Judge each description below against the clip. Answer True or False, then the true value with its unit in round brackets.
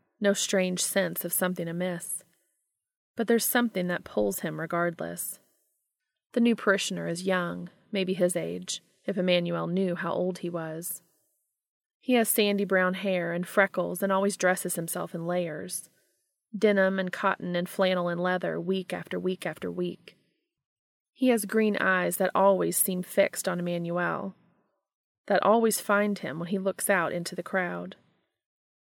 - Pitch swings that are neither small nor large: False (2.3 semitones)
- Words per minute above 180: False (155 wpm)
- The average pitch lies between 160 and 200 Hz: True (185 Hz)